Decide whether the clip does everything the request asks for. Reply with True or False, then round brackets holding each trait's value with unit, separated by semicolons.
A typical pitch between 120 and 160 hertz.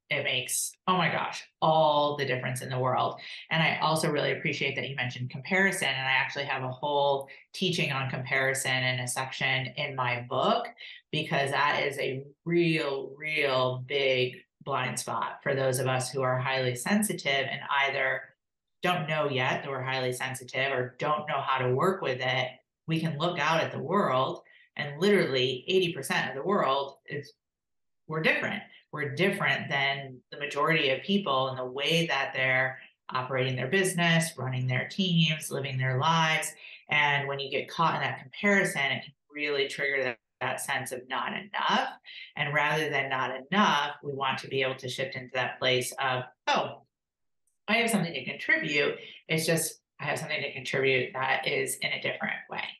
True (140 Hz)